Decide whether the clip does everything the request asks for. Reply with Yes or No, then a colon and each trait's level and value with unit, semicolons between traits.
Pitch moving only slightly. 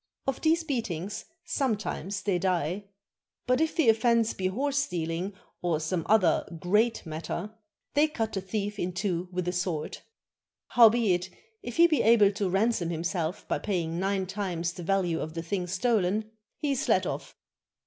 No: average, 4.3 semitones